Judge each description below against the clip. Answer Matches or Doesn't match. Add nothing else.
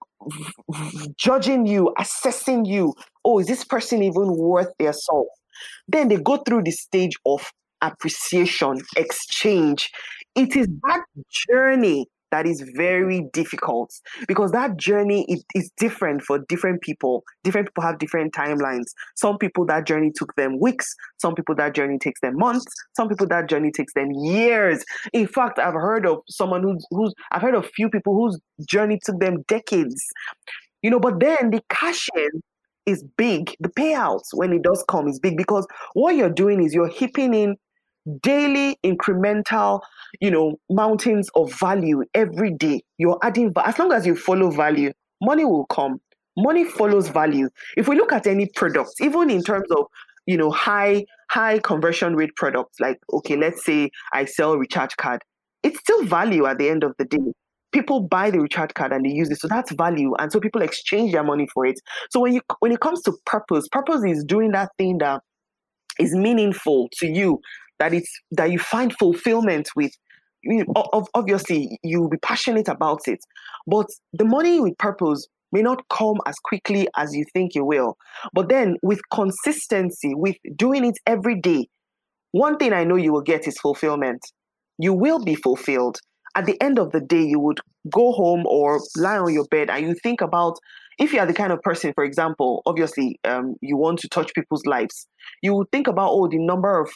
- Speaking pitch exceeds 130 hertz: Matches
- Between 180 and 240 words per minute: Matches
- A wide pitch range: Matches